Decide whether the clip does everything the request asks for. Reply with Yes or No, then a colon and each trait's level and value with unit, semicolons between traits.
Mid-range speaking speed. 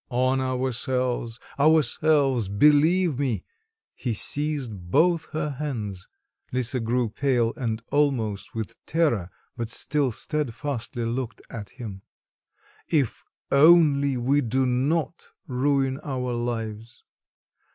No: slow, 105 wpm